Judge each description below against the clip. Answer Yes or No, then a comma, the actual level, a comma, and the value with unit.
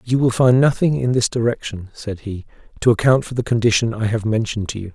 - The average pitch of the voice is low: Yes, low, 115 Hz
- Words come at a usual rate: No, fast, 230 wpm